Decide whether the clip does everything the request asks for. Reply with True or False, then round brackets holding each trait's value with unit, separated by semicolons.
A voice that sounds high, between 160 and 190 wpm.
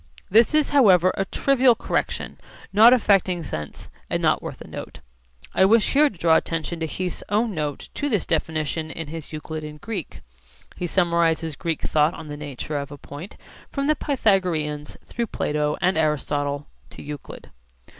False (165 Hz; 170 wpm)